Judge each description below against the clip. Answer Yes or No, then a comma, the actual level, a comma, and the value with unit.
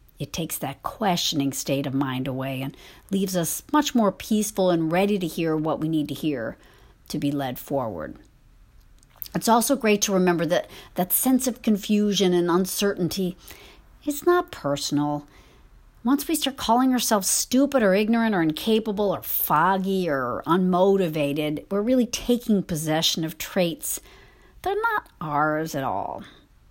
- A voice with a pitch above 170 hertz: Yes, medium, 185 Hz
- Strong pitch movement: Yes, wide, 6.0 semitones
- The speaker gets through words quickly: No, average, 155 wpm